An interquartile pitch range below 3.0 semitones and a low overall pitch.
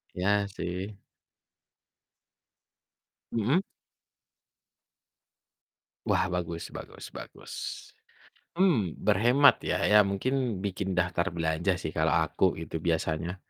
No: average, 3.6 semitones; very low, 95 Hz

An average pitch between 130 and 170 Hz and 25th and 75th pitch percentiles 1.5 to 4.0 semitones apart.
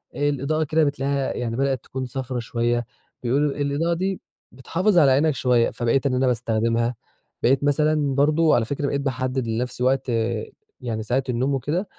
Yes: low, 135 Hz; average, 2.8 semitones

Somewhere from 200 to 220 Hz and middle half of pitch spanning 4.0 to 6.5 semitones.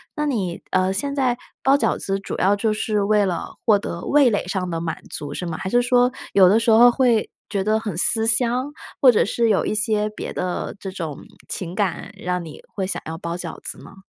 Yes: high, 205 Hz; average, 4.3 semitones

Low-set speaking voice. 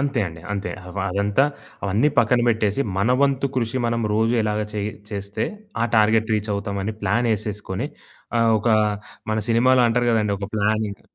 Yes: low, 110 Hz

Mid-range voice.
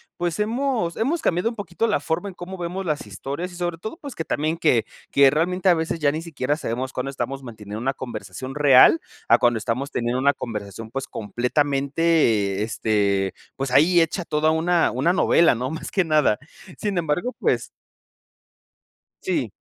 Yes: medium, 150 Hz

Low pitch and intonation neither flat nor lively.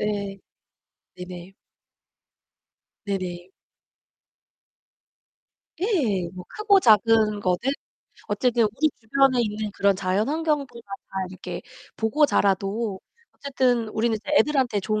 No: high, 215 Hz; average, 4.7 semitones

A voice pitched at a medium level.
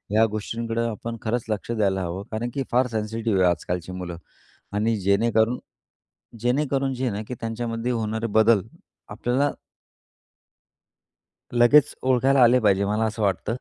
No: low, 115 Hz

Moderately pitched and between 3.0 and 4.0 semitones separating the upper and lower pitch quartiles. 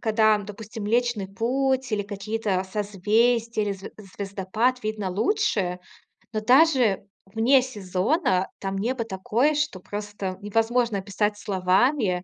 No: high, 215 Hz; average, 3.6 semitones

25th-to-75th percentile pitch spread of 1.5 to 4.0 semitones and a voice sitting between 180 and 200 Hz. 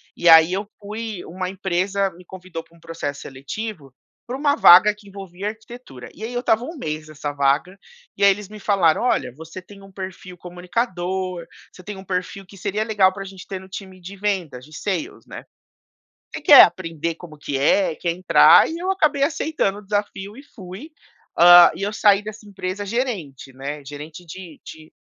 Yes: average, 3.7 semitones; high, 190 Hz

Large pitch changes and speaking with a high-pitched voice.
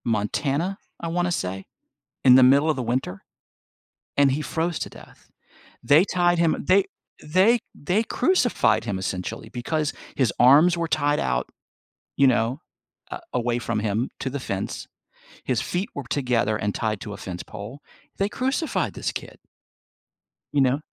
No: wide, 7.0 semitones; low, 135 Hz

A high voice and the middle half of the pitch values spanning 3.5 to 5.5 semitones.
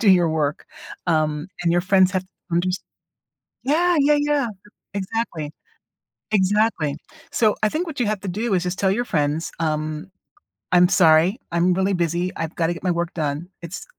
No: medium, 180 Hz; average, 4.0 semitones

